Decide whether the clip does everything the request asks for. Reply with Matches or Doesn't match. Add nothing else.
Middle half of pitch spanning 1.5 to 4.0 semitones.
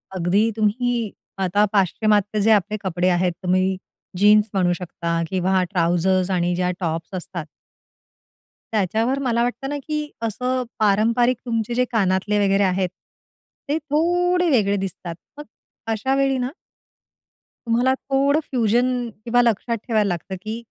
Doesn't match